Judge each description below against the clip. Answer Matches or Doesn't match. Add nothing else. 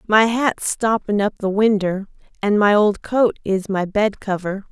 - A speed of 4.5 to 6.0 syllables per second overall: Doesn't match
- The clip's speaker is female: Matches